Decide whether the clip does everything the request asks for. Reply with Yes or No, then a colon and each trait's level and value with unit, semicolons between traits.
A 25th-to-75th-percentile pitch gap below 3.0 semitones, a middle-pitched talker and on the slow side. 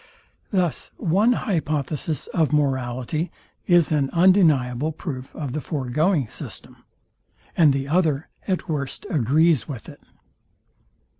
No: average, 3.9 semitones; medium, 150 Hz; slow, 115 wpm